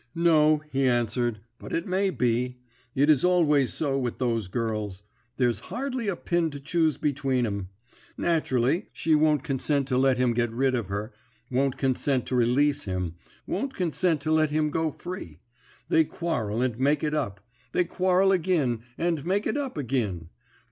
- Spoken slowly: No, average, 170 wpm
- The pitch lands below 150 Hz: Yes, medium, 140 Hz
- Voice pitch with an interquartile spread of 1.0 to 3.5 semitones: No, average, 5.2 semitones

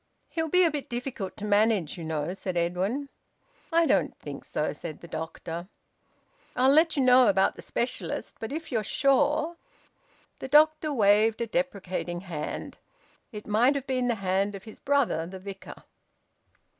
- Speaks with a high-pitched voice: Yes, high, 225 Hz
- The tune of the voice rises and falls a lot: Yes, wide, 6.6 semitones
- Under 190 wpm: Yes, average, 170 wpm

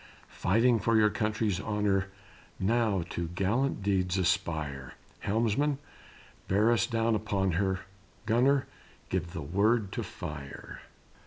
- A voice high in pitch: No, low, 100 Hz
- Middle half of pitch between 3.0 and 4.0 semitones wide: Yes, average, 3.5 semitones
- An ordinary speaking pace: No, slow, 115 wpm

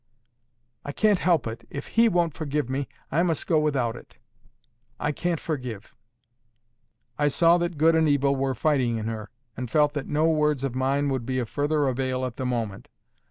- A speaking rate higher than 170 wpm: Yes, average, 190 wpm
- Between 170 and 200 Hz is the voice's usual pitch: No, medium, 145 Hz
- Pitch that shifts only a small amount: No, average, 3.5 semitones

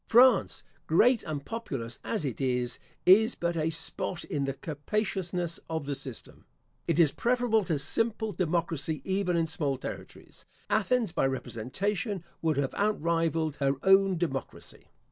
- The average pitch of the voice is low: No, medium, 165 Hz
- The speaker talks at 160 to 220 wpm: No, average, 145 wpm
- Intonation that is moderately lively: No, wide, 5.8 semitones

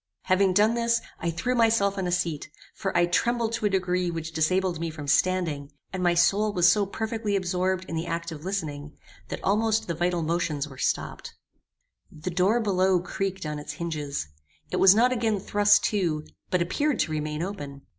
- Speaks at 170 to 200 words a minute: Yes, average, 190 wpm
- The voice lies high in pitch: No, medium, 180 Hz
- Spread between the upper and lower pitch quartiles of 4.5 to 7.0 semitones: No, average, 3.6 semitones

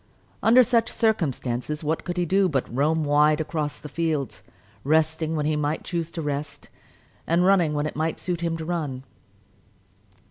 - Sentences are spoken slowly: No, average, 175 wpm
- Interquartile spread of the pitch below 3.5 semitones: Yes, narrow, 2.6 semitones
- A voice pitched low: No, medium, 155 Hz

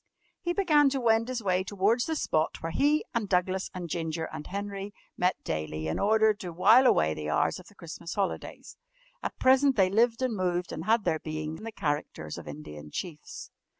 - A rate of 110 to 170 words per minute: No, average, 200 wpm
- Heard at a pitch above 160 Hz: Yes, high, 190 Hz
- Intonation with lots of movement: Yes, wide, 6.1 semitones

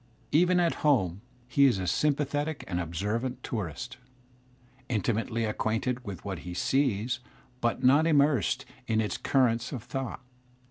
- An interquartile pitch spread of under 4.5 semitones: No, average, 5.0 semitones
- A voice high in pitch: No, low, 120 Hz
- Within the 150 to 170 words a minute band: No, slow, 135 wpm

